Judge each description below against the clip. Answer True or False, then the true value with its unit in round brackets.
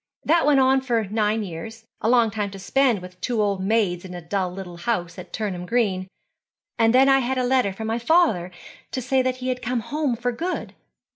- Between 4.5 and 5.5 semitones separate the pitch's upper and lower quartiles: True (4.9 semitones)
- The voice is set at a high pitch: True (225 Hz)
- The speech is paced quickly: True (215 wpm)